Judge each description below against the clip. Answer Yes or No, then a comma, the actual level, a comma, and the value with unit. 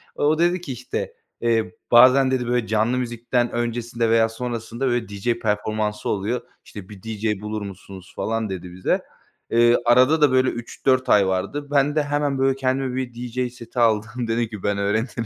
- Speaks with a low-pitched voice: Yes, low, 120 Hz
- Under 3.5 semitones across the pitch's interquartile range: Yes, average, 3.0 semitones